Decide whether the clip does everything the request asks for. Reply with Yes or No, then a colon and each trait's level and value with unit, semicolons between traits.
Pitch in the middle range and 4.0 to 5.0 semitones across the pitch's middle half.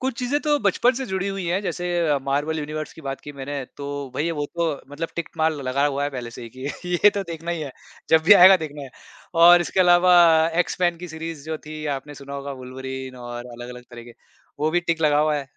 Yes: medium, 155 Hz; average, 4.3 semitones